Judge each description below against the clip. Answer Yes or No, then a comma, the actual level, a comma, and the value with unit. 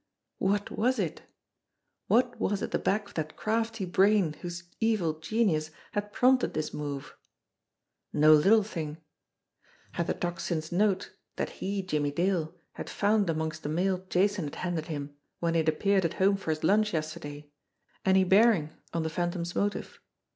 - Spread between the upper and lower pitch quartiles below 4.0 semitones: No, average, 4.5 semitones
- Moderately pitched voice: Yes, medium, 175 Hz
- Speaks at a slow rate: No, average, 165 wpm